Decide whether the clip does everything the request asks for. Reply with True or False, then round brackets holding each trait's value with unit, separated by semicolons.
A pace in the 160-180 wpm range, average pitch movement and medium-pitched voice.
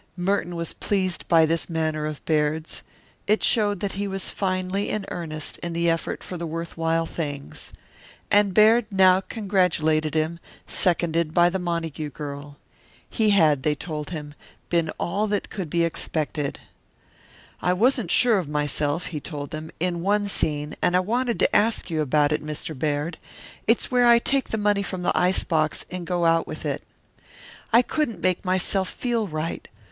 True (175 wpm; 4.1 semitones; 170 Hz)